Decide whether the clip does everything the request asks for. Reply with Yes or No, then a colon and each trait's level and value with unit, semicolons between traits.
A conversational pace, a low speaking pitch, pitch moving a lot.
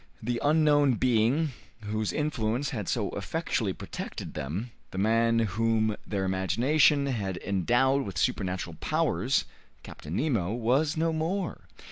No: slow, 125 wpm; low, 115 Hz; wide, 6.2 semitones